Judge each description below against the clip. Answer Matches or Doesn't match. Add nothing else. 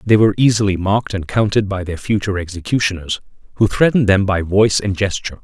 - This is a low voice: Matches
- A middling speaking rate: Matches